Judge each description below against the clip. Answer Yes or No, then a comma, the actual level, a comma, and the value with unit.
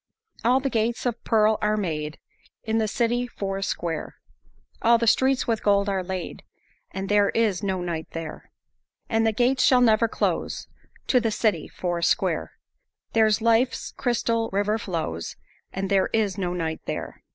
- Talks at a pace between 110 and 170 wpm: Yes, average, 165 wpm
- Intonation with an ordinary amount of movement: Yes, average, 3.4 semitones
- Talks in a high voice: Yes, high, 215 Hz